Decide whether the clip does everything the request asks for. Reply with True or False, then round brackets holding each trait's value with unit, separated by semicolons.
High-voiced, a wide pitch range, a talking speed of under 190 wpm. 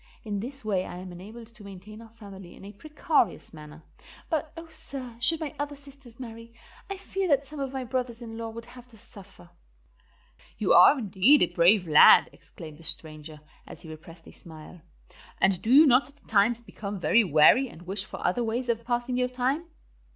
False (230 Hz; 5.7 semitones; 200 wpm)